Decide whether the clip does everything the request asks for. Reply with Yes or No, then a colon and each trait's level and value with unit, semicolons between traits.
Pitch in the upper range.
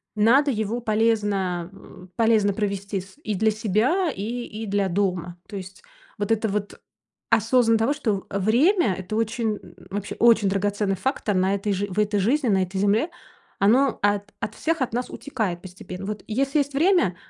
Yes: high, 210 Hz